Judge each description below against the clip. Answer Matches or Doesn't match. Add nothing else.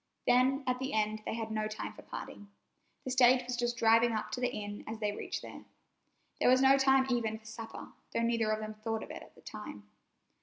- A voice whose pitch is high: Matches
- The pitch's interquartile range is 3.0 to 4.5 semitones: Doesn't match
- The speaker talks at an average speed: Doesn't match